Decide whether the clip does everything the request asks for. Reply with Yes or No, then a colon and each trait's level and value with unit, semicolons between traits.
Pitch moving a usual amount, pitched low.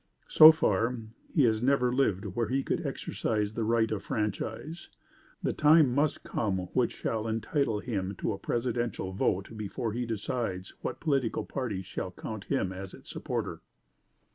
Yes: average, 3.8 semitones; low, 115 Hz